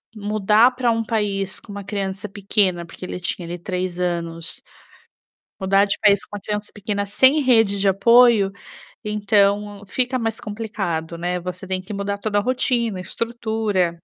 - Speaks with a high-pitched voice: Yes, high, 200 Hz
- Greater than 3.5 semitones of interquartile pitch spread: No, average, 2.8 semitones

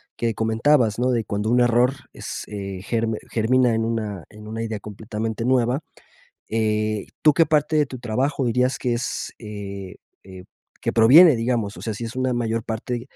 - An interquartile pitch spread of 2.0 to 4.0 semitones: Yes, average, 2.7 semitones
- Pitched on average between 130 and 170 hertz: No, low, 115 Hz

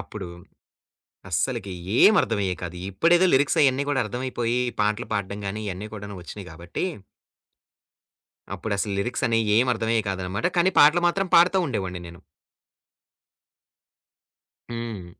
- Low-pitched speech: Yes, low, 110 Hz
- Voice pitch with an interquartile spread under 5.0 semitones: No, average, 5.3 semitones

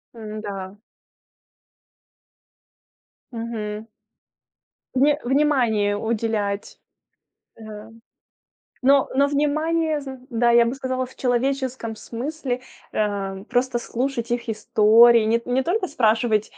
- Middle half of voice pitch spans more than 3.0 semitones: Yes, average, 3.6 semitones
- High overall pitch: Yes, high, 235 Hz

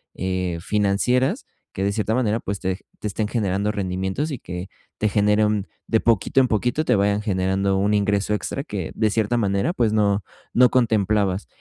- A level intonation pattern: Yes, narrow, 2.2 semitones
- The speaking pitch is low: Yes, low, 105 Hz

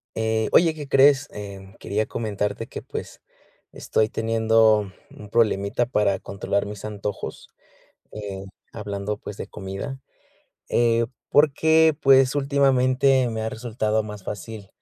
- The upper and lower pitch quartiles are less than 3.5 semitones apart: No, average, 4.0 semitones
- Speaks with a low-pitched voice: Yes, low, 110 Hz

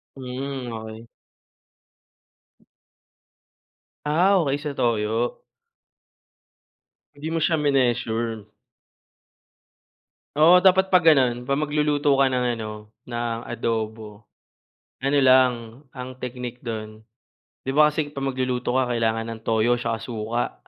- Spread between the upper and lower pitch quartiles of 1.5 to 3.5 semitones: No, average, 3.9 semitones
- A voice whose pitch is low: Yes, low, 125 Hz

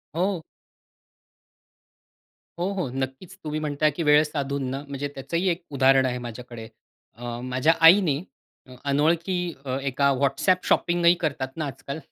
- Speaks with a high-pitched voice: No, medium, 145 Hz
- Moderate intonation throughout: Yes, average, 4.0 semitones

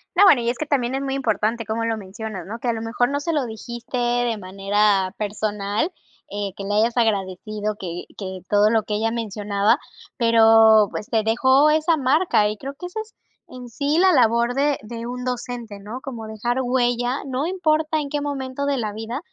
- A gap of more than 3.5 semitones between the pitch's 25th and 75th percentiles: Yes, average, 4.0 semitones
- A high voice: Yes, high, 235 Hz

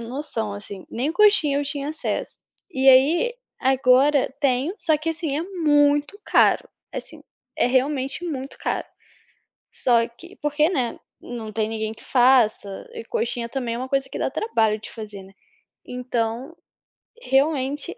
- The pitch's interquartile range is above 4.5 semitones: No, average, 4.2 semitones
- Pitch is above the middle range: Yes, very high, 270 Hz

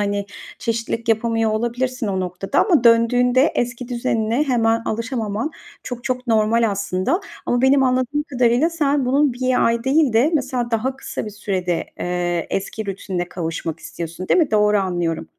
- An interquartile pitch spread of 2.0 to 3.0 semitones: No, average, 4.0 semitones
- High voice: Yes, high, 230 Hz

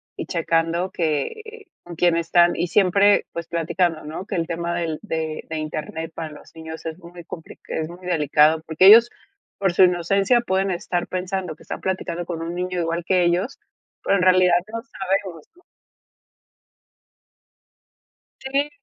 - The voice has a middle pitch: Yes, medium, 175 Hz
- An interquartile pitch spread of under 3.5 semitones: Yes, narrow, 2.5 semitones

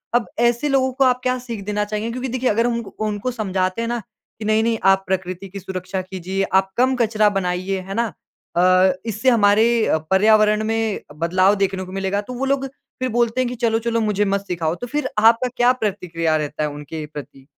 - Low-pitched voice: No, high, 210 Hz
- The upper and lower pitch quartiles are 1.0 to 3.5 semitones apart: No, average, 3.9 semitones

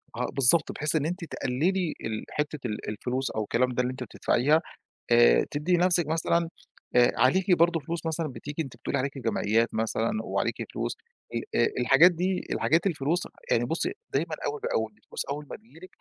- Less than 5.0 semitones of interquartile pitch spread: No, wide, 5.6 semitones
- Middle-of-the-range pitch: Yes, medium, 150 Hz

